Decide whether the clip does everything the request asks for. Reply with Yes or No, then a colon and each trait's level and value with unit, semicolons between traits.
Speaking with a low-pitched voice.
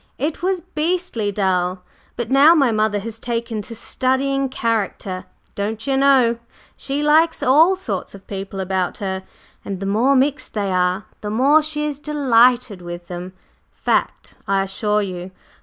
No: high, 230 Hz